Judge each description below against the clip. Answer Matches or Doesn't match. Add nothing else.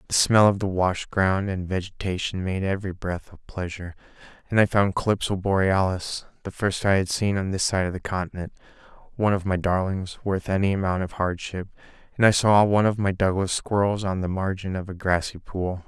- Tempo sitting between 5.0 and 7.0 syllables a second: Matches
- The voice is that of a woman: Doesn't match